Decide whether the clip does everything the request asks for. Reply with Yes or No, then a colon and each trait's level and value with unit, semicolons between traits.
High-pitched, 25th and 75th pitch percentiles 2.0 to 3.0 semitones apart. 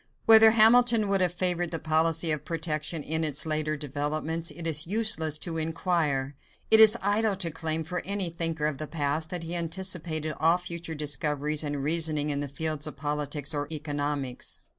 No: medium, 160 Hz; average, 2.7 semitones